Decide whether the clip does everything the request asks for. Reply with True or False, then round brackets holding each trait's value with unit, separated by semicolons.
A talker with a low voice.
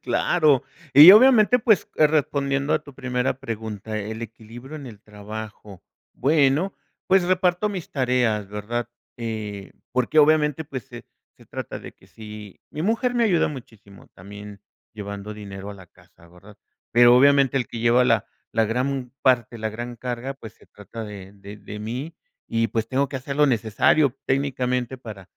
True (120 Hz)